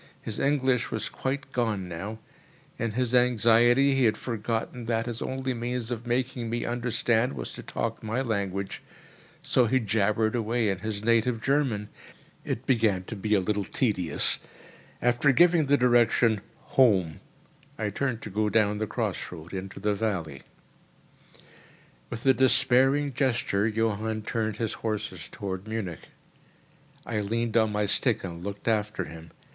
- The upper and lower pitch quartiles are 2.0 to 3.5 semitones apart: Yes, average, 2.9 semitones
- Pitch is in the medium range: No, low, 115 Hz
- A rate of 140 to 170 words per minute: Yes, average, 150 wpm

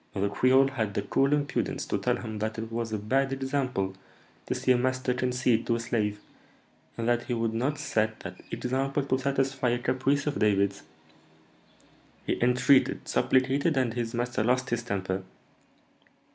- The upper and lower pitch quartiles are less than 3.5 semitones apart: Yes, average, 3.1 semitones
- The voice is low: Yes, low, 125 Hz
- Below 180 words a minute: Yes, average, 170 wpm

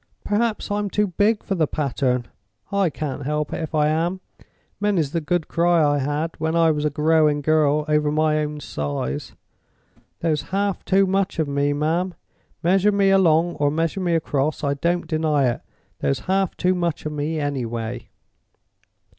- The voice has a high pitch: No, medium, 155 Hz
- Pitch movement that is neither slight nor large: Yes, average, 3.3 semitones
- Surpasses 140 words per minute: Yes, average, 165 wpm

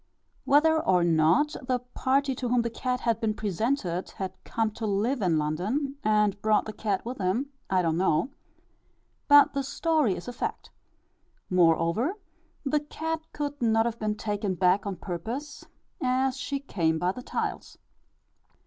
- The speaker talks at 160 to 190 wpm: Yes, average, 165 wpm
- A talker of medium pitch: No, high, 225 Hz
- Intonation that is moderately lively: No, wide, 6.3 semitones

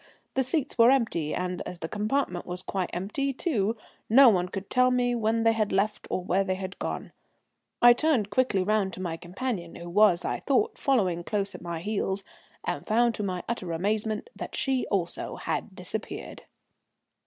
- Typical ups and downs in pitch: Yes, average, 4.9 semitones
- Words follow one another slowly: No, average, 185 wpm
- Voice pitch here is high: Yes, high, 210 Hz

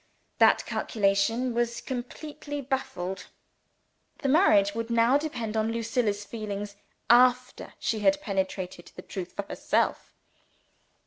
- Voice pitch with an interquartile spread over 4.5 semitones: No, average, 3.9 semitones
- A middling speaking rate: No, slow, 130 wpm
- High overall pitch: Yes, high, 230 Hz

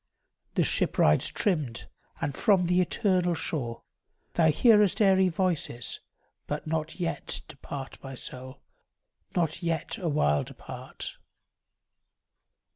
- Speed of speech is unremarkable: No, slow, 110 wpm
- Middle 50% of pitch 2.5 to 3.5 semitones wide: No, average, 5.3 semitones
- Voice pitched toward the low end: No, medium, 165 Hz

